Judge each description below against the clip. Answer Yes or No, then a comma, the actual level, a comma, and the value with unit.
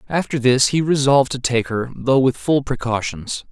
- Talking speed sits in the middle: Yes, average, 190 wpm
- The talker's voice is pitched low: Yes, low, 130 Hz